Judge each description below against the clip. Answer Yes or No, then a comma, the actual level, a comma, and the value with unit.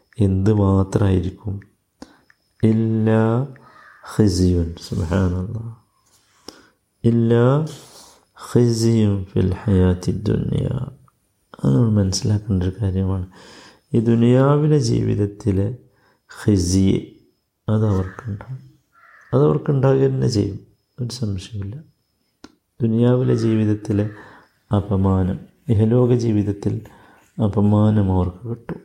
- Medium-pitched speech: No, low, 105 Hz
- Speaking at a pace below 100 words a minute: Yes, slow, 60 wpm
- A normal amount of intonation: Yes, average, 3.3 semitones